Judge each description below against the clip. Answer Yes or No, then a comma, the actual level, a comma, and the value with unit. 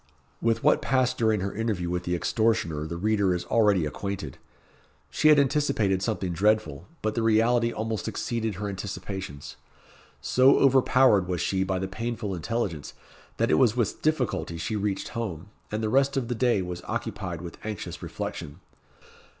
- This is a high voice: No, low, 105 Hz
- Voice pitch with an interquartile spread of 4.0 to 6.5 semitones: Yes, average, 4.4 semitones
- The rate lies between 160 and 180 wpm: Yes, average, 165 wpm